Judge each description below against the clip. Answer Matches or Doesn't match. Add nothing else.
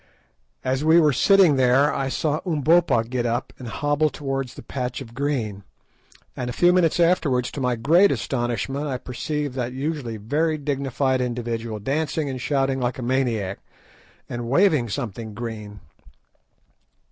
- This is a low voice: Matches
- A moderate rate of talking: Matches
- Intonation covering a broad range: Doesn't match